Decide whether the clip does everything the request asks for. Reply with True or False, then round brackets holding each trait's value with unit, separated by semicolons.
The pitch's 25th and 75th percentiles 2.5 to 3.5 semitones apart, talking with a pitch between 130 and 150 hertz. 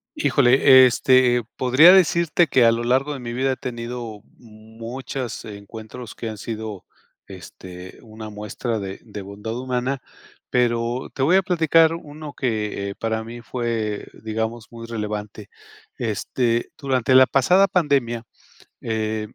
False (3.2 semitones; 120 Hz)